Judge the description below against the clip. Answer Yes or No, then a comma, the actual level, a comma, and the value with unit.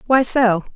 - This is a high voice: Yes, high, 230 Hz